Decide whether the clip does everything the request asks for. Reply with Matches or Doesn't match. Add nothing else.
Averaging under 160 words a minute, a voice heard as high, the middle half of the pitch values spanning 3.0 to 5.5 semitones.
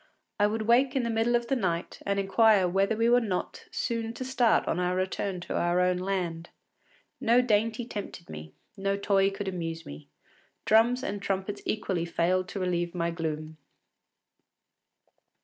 Doesn't match